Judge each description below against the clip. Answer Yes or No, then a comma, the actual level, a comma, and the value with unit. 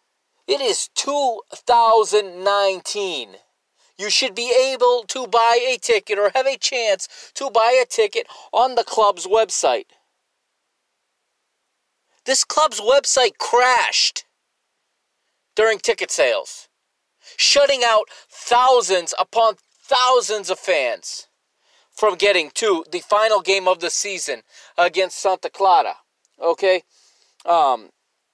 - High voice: Yes, high, 235 Hz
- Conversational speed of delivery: No, slow, 110 wpm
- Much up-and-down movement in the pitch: Yes, wide, 5.7 semitones